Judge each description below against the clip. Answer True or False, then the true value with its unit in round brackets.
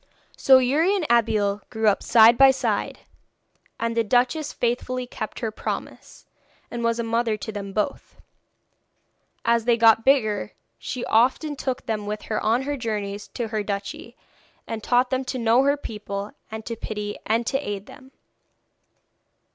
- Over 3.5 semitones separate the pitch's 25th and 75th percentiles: False (3.0 semitones)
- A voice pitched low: False (230 Hz)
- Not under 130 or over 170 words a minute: True (165 wpm)